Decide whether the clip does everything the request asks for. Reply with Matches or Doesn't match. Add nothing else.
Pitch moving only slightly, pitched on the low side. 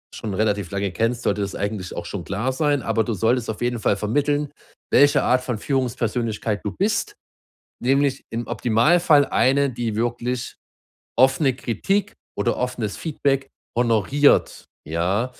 Doesn't match